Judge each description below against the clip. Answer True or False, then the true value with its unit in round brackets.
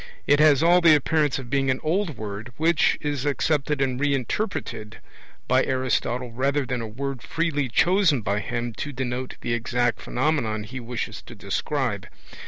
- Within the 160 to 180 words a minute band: True (170 wpm)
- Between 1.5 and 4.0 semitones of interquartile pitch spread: True (3.5 semitones)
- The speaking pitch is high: False (135 Hz)